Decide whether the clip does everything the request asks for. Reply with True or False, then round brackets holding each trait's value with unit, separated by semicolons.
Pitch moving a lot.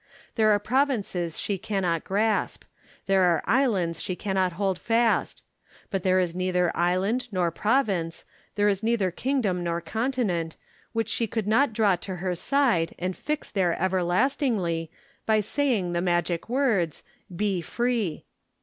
False (4.4 semitones)